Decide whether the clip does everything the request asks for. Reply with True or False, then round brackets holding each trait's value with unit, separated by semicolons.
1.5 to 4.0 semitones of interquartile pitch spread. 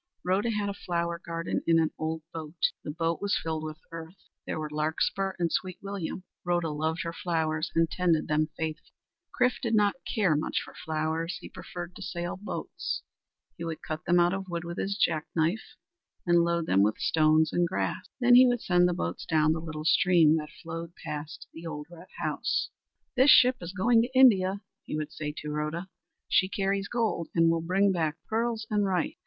True (3.4 semitones)